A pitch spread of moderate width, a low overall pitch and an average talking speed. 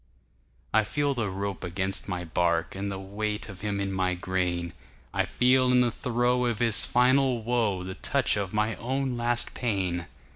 Yes: average, 4.6 semitones; low, 105 Hz; average, 160 wpm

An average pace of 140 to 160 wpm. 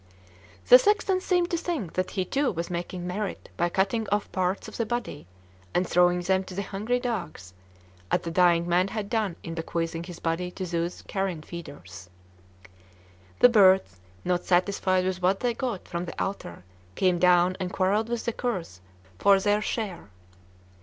No: average, 175 wpm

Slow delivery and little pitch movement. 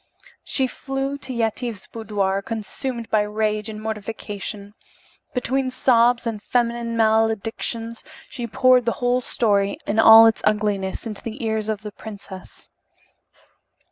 Yes: slow, 130 wpm; narrow, 2.2 semitones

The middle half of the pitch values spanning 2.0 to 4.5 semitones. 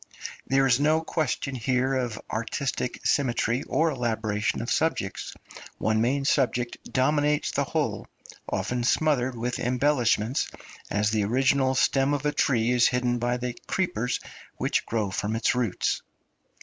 Yes: average, 2.9 semitones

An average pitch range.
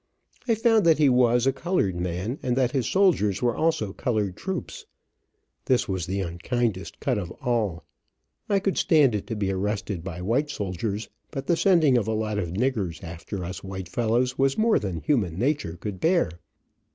No: wide, 6.3 semitones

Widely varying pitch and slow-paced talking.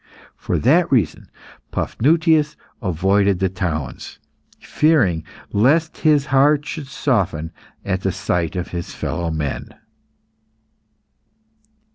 Yes: wide, 9.0 semitones; slow, 100 wpm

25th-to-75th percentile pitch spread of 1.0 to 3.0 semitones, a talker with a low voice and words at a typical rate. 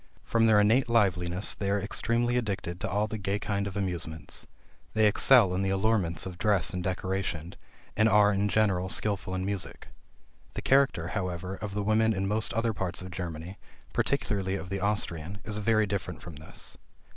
Yes: narrow, 2.6 semitones; low, 100 Hz; average, 180 wpm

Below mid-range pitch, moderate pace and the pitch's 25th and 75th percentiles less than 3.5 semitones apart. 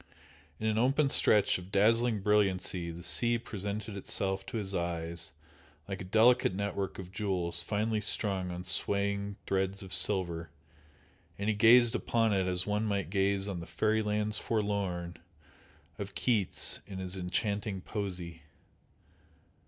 Yes: low, 100 Hz; average, 145 wpm; narrow, 2.4 semitones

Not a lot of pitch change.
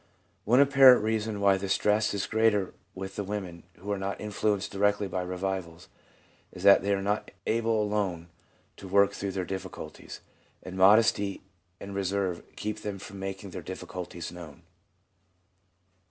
Yes: narrow, 1.9 semitones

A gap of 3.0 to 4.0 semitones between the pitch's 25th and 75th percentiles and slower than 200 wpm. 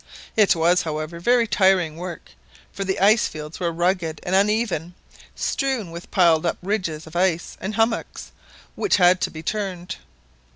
Yes: average, 3.4 semitones; average, 160 wpm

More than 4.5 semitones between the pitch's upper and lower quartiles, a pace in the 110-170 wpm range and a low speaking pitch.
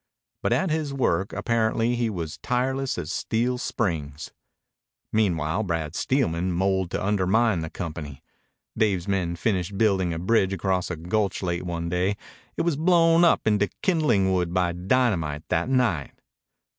Yes: average, 5.3 semitones; average, 150 wpm; very low, 95 Hz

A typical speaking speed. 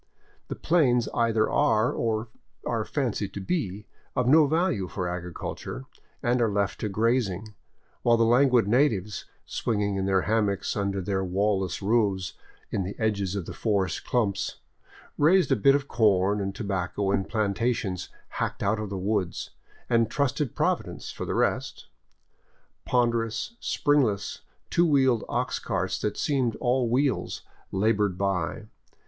Yes: average, 145 wpm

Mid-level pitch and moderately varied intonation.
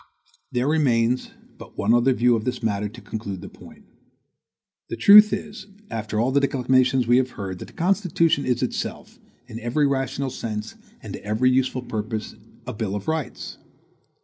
No: low, 125 Hz; average, 3.3 semitones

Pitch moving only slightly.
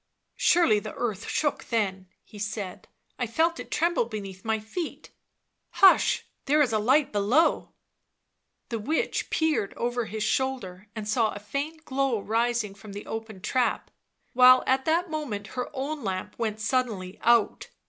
No: average, 4.6 semitones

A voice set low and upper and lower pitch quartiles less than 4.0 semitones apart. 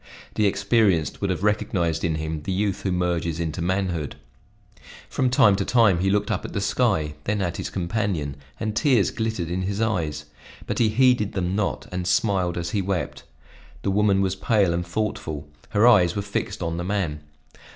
Yes: very low, 95 Hz; average, 3.4 semitones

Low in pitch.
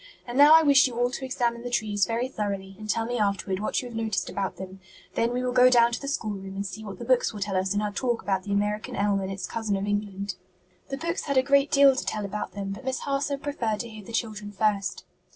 No: high, 220 Hz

